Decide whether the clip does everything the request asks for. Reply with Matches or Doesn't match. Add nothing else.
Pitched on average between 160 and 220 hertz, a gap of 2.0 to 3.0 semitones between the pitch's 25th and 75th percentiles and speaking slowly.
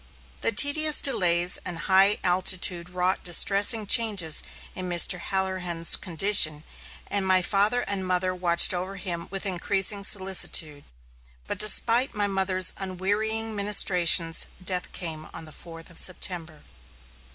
Matches